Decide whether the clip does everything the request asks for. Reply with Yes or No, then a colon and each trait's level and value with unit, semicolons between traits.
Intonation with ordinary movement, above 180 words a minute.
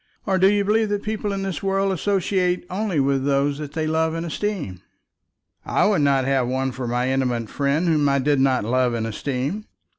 No: wide, 6.5 semitones; average, 200 wpm